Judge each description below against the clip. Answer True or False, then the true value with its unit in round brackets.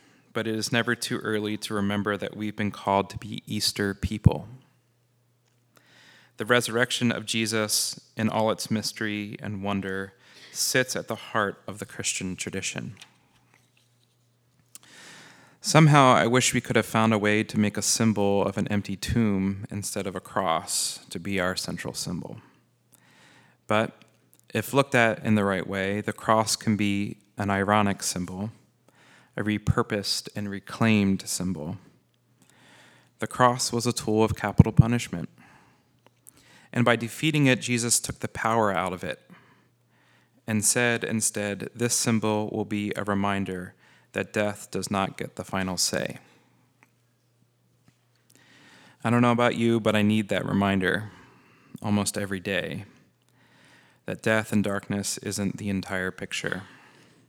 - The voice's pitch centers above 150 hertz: False (110 Hz)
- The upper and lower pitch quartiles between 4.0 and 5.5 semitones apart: False (3.0 semitones)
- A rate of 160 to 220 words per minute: False (145 wpm)